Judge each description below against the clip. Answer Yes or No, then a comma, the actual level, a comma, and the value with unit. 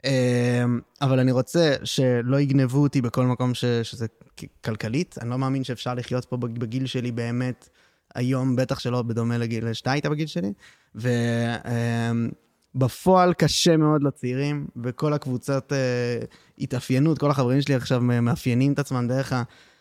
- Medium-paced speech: Yes, average, 135 wpm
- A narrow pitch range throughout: Yes, narrow, 2.2 semitones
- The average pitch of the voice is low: Yes, low, 125 Hz